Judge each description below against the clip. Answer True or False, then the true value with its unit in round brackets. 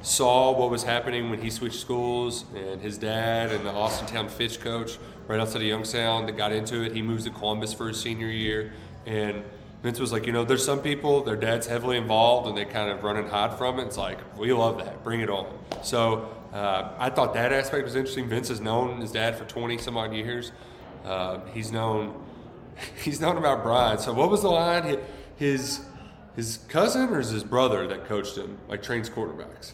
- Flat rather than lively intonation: True (2.0 semitones)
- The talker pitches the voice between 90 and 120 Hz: True (115 Hz)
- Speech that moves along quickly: True (215 wpm)